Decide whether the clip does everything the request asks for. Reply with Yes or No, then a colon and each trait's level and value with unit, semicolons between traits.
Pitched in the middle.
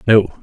No: low, 105 Hz